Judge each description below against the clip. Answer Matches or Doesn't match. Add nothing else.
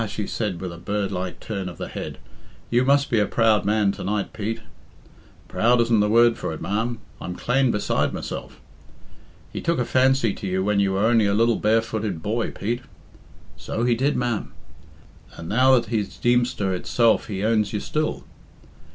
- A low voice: Matches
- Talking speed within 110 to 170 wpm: Doesn't match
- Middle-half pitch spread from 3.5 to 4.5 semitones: Doesn't match